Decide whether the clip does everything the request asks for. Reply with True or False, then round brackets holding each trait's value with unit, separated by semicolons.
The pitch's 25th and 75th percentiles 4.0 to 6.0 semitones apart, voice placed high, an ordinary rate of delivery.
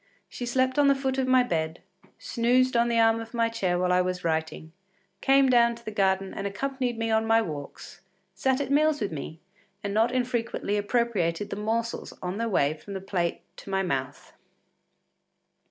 True (5.1 semitones; 225 Hz; 190 wpm)